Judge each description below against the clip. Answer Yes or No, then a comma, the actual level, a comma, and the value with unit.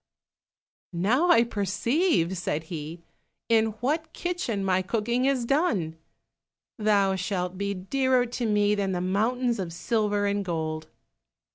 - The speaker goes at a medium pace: No, slow, 130 wpm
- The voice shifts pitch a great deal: No, average, 4.9 semitones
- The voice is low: No, high, 205 Hz